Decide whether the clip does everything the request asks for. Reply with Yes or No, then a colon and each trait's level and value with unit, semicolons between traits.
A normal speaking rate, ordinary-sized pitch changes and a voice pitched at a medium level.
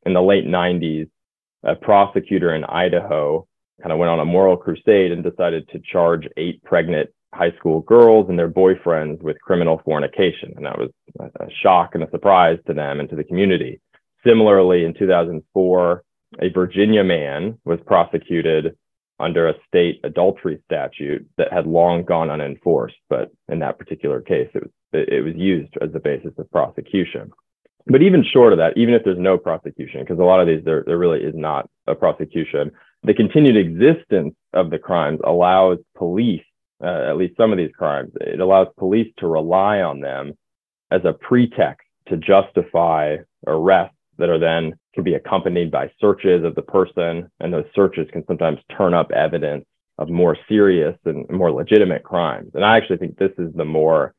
No: average, 175 wpm; average, 3.3 semitones; very low, 90 Hz